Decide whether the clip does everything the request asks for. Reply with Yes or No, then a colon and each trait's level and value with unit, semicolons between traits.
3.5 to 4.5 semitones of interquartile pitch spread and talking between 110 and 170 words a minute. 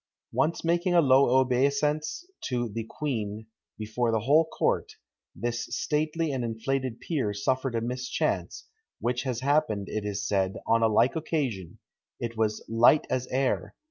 Yes: average, 4.1 semitones; average, 150 wpm